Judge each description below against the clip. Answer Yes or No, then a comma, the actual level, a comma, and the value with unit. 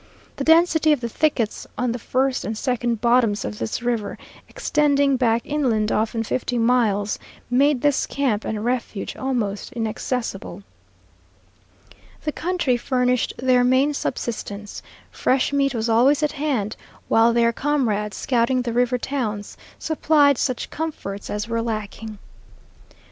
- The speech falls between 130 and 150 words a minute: Yes, slow, 135 wpm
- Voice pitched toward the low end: No, high, 245 Hz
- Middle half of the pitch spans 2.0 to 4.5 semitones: Yes, average, 3.8 semitones